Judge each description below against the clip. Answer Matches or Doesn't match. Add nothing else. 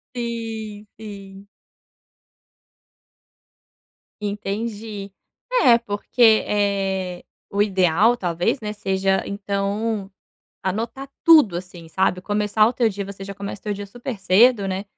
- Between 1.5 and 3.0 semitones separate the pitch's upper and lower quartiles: Matches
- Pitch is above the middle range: Matches